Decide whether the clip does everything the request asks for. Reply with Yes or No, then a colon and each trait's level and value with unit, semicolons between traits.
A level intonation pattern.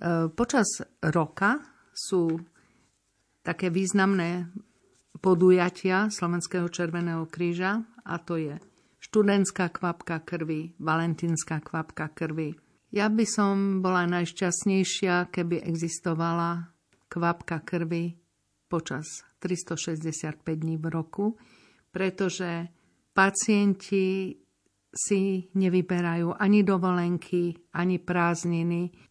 Yes: narrow, 2.3 semitones